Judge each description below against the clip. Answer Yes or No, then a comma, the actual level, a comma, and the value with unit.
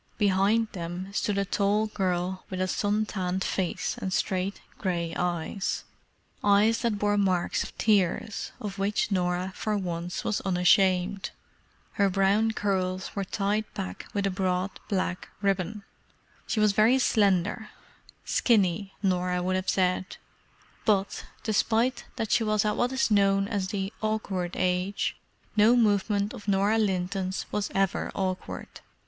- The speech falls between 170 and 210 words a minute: No, slow, 135 wpm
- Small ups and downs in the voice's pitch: Yes, narrow, 2.2 semitones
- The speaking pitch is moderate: No, high, 195 Hz